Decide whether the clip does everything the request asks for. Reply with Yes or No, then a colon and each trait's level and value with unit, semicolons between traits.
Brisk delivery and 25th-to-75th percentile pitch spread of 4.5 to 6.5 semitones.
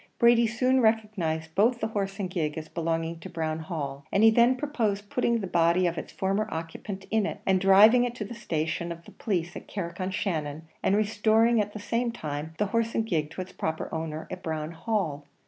Yes: fast, 215 wpm; average, 5.3 semitones